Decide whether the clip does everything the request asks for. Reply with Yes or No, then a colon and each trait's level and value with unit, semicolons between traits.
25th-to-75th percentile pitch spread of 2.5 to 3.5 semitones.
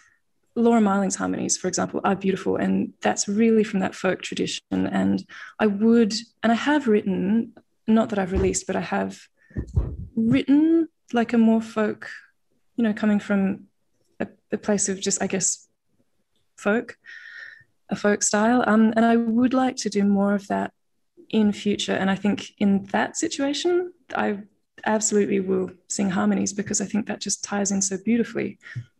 Yes: average, 2.8 semitones